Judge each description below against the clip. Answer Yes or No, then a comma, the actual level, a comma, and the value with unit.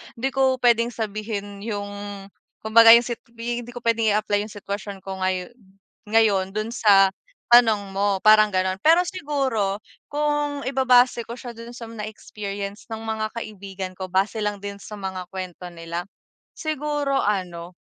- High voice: Yes, high, 215 Hz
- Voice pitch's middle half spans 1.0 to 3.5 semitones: Yes, average, 3.2 semitones